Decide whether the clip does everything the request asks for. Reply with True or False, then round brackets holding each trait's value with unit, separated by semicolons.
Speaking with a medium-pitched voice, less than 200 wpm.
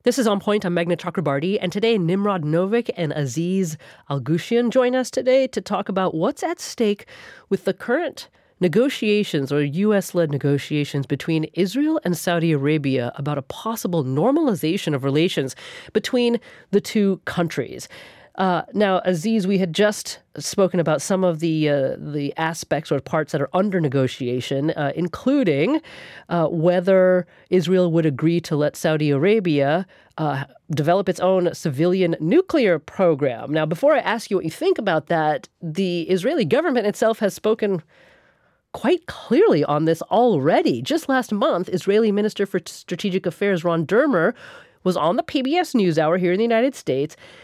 True (180 Hz; 160 wpm)